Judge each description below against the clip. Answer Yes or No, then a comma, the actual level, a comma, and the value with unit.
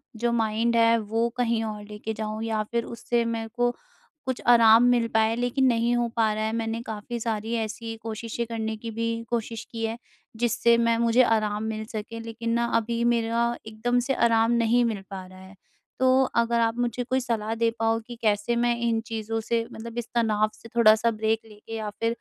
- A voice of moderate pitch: No, high, 230 Hz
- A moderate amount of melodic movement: No, narrow, 1.3 semitones